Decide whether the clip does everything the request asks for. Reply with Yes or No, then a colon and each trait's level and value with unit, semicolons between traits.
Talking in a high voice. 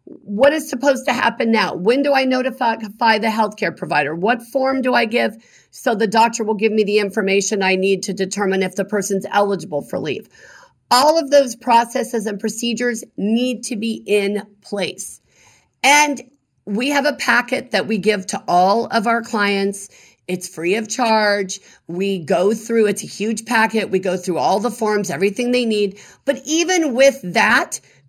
Yes: high, 220 Hz